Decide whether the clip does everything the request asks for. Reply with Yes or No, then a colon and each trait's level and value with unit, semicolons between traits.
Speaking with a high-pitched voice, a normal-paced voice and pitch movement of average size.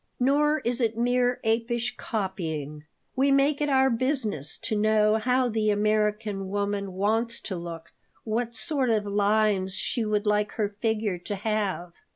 Yes: high, 215 Hz; average, 155 wpm; average, 3.1 semitones